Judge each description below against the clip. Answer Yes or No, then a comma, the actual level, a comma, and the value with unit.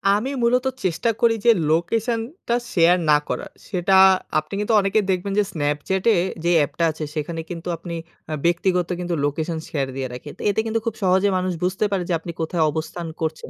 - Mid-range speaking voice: Yes, medium, 180 Hz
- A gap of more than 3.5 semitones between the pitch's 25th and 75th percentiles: Yes, average, 4.1 semitones